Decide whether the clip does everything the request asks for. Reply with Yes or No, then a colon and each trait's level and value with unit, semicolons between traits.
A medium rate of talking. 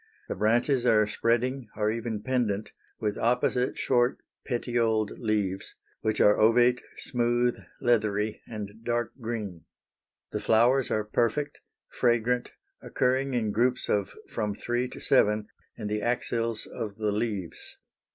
No: slow, 130 wpm